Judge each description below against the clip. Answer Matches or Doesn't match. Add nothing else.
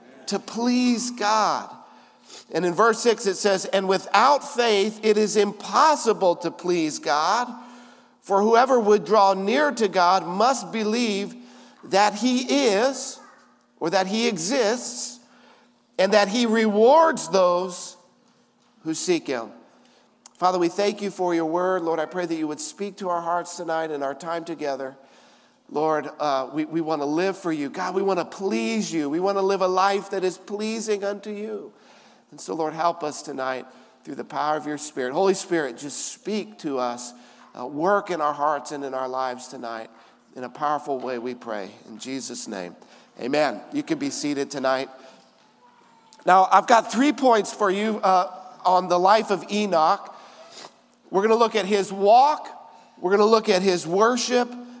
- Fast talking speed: Doesn't match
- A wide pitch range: Matches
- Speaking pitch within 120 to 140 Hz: Doesn't match